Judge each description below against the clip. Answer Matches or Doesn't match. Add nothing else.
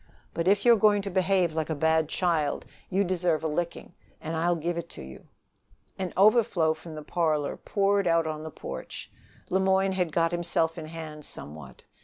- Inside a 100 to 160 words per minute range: Doesn't match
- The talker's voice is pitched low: Doesn't match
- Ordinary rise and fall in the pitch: Matches